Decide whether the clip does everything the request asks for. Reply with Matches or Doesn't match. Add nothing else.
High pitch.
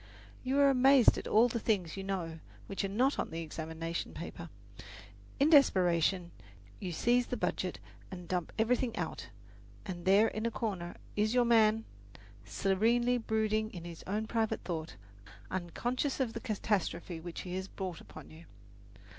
Matches